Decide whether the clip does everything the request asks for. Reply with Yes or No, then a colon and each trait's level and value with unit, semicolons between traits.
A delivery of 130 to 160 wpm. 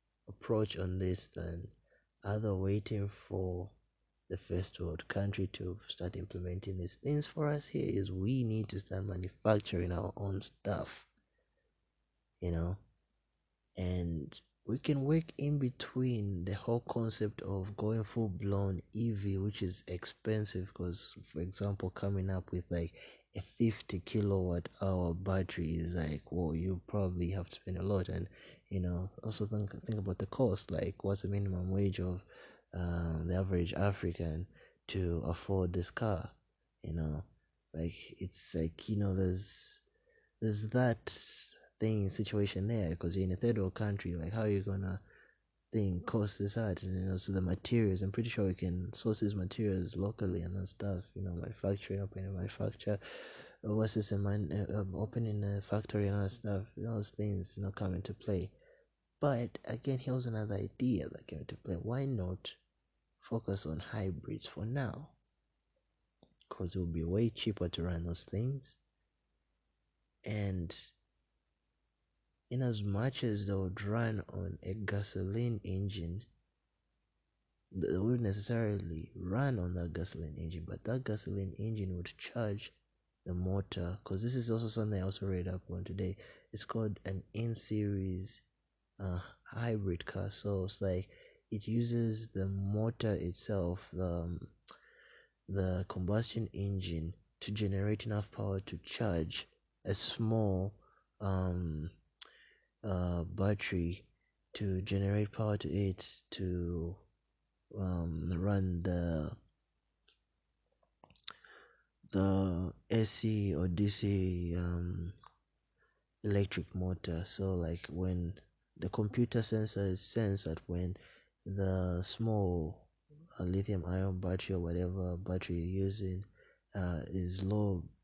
Yes: average, 140 wpm